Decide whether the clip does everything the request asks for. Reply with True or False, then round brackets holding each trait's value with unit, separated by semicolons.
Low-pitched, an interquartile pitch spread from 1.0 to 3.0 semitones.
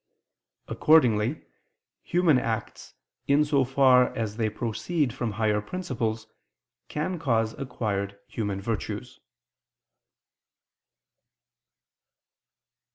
False (120 Hz; 4.5 semitones)